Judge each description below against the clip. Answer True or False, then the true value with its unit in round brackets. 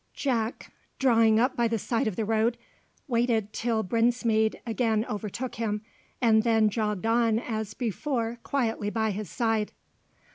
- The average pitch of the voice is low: False (225 Hz)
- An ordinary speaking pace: True (145 wpm)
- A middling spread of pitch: False (1.5 semitones)